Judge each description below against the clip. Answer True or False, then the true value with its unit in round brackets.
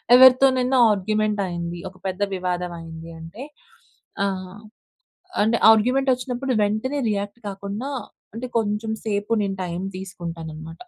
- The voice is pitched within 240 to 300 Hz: False (205 Hz)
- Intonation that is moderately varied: True (4.5 semitones)